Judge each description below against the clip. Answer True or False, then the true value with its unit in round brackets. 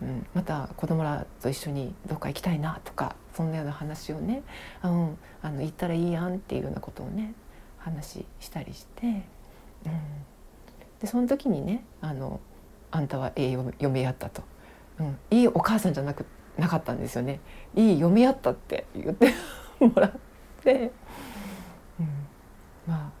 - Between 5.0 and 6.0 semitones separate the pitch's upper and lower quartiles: True (5.5 semitones)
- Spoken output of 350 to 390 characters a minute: False (305 characters per minute)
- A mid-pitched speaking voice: True (160 Hz)